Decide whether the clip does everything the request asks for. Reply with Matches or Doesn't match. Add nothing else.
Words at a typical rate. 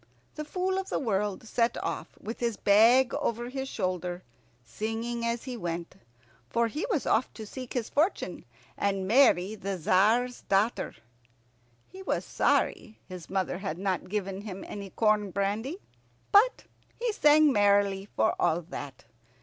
Matches